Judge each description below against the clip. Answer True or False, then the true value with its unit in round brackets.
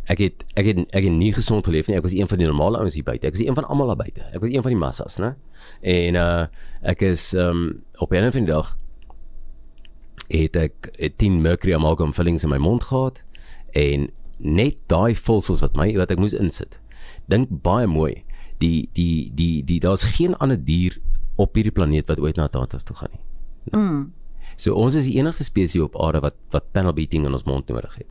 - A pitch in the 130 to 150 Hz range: False (90 Hz)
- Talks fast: True (220 wpm)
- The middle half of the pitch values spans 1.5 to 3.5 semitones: False (5.7 semitones)